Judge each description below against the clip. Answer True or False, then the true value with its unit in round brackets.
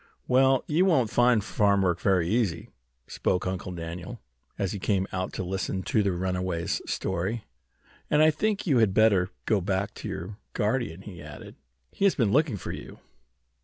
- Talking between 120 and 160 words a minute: False (175 wpm)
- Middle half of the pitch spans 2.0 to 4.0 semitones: False (4.8 semitones)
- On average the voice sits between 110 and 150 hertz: False (100 Hz)